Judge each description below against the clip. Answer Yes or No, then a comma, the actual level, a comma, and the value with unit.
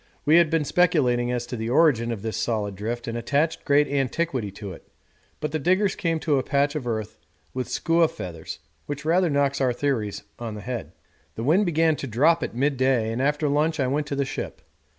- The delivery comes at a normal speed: No, fast, 210 wpm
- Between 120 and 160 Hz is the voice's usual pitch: Yes, medium, 140 Hz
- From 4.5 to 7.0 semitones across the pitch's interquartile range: Yes, average, 4.8 semitones